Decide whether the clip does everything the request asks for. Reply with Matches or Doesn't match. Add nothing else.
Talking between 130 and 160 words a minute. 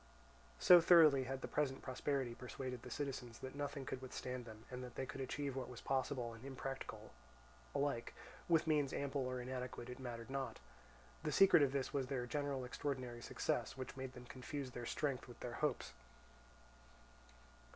Doesn't match